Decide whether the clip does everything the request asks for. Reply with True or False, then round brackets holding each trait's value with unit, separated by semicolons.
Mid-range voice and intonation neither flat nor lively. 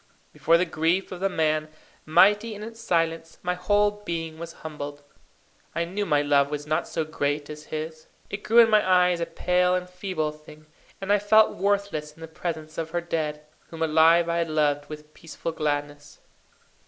True (165 Hz; 3.0 semitones)